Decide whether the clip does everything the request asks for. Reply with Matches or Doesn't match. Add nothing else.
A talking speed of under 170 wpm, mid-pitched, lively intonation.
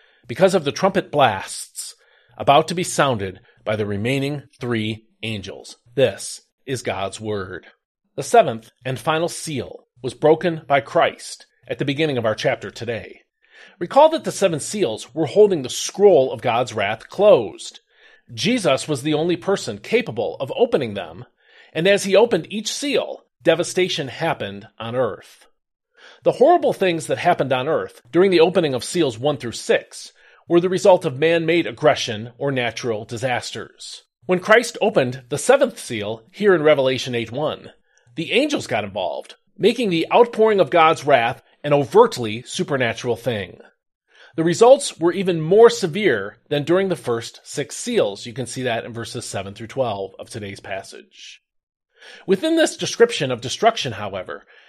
Matches